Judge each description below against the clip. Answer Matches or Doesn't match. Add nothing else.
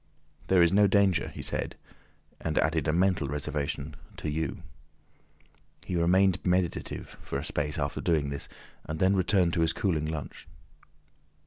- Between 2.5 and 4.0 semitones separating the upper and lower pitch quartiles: Matches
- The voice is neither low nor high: Doesn't match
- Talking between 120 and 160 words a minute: Matches